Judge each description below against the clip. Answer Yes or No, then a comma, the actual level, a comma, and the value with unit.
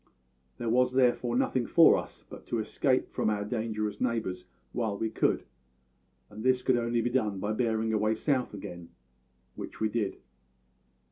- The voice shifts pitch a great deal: No, narrow, 2.5 semitones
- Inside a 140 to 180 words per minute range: Yes, average, 160 wpm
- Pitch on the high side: No, low, 115 Hz